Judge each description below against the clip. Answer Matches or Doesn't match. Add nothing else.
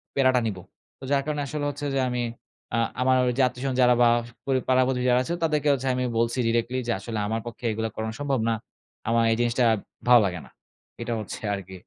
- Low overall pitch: Matches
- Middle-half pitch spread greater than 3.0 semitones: Doesn't match